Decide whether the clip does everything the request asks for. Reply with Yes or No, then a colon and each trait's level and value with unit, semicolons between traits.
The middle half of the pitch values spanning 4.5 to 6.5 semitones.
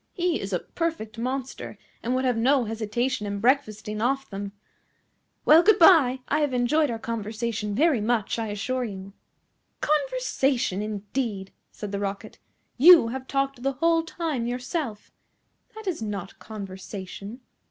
Yes: average, 4.9 semitones